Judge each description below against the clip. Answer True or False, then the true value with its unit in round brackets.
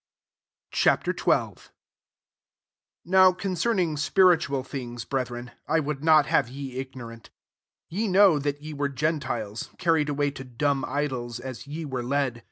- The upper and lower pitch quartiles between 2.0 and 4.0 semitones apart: True (3.7 semitones)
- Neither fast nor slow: True (155 wpm)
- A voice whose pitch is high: False (145 Hz)